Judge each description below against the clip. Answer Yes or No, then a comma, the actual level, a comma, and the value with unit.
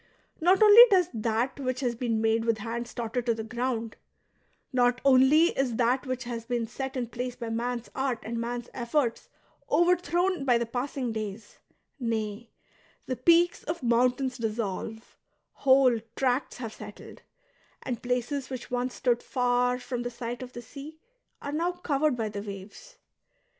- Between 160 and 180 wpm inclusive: Yes, average, 165 wpm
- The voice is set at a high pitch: Yes, high, 245 Hz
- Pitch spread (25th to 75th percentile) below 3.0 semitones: Yes, narrow, 2.6 semitones